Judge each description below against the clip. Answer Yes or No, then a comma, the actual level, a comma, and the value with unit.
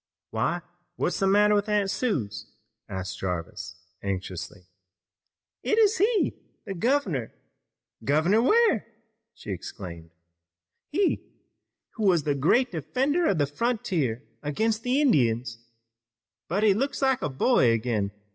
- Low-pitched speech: No, medium, 175 Hz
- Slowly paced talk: Yes, slow, 120 wpm